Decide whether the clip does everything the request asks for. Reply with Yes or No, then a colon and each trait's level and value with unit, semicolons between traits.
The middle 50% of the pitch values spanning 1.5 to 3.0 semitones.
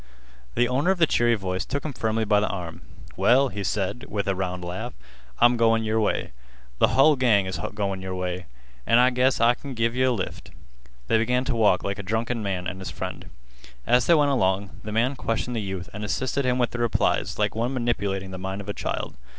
No: average, 4.2 semitones